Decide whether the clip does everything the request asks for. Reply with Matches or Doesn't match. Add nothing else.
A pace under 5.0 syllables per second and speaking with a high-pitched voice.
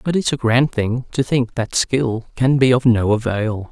Doesn't match